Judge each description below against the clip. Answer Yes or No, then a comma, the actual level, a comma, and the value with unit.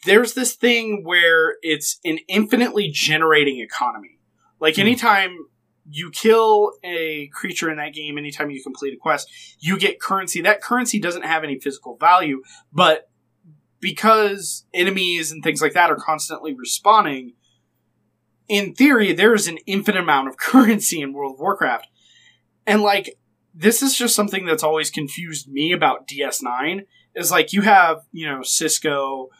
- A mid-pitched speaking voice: Yes, medium, 165 Hz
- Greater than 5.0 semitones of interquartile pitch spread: Yes, wide, 5.6 semitones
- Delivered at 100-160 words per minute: Yes, average, 150 wpm